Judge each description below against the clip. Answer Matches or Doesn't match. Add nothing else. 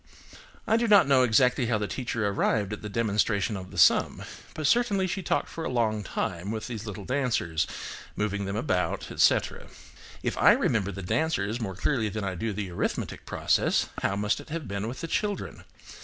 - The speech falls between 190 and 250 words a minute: Matches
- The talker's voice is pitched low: Matches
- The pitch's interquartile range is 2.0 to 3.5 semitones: Doesn't match